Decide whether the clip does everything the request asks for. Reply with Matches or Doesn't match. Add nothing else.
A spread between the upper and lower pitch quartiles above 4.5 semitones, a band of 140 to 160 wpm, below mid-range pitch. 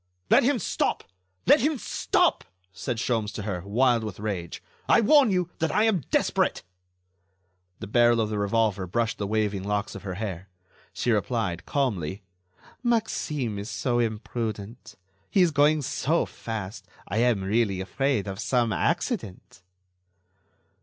Matches